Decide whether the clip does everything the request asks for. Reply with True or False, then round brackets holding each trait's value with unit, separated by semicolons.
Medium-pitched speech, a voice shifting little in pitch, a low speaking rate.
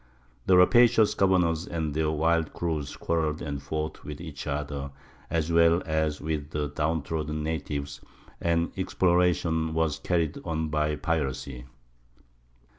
False (80 Hz; 1.9 semitones; 125 wpm)